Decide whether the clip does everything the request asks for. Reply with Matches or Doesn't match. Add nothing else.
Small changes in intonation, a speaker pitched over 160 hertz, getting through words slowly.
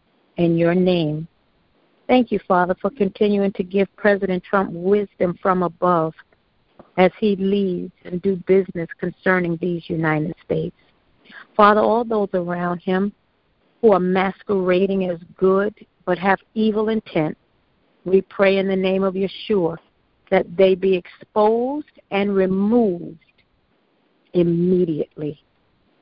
Matches